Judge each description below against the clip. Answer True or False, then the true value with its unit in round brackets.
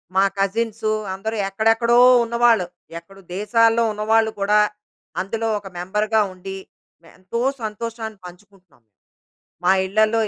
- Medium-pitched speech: False (215 Hz)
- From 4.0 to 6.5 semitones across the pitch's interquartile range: False (2.5 semitones)